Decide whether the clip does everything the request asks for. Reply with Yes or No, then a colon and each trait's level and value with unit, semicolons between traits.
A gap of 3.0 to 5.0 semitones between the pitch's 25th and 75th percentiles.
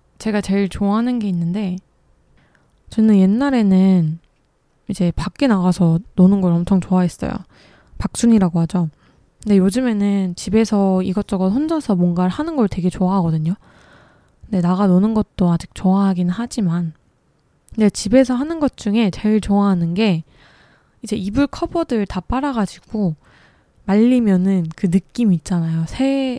Yes: average, 3.5 semitones